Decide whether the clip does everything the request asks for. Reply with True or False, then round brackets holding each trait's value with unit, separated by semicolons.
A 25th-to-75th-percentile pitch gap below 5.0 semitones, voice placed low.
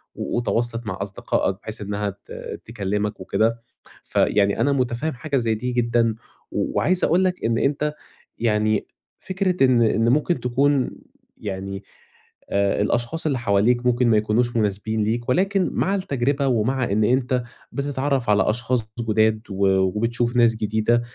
True (3.4 semitones; 115 Hz)